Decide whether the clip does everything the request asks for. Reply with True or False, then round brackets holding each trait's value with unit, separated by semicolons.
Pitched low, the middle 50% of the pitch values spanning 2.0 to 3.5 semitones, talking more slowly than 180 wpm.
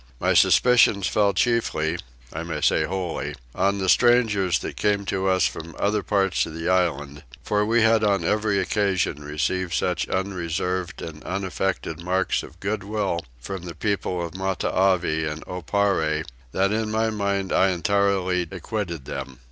True (95 Hz; 3.2 semitones; 155 wpm)